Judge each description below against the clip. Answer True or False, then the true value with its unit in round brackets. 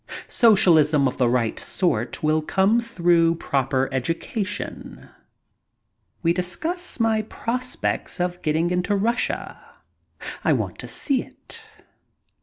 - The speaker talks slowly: True (110 wpm)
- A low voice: False (175 Hz)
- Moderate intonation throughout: False (6.4 semitones)